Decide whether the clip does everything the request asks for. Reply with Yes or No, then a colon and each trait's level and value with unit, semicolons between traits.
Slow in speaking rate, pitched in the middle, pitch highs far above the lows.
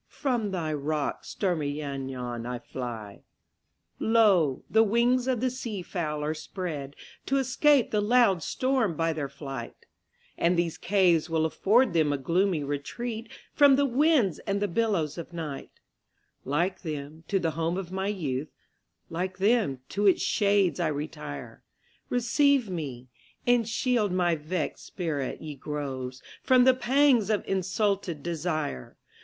Yes: slow, 130 wpm; medium, 175 Hz; wide, 6.9 semitones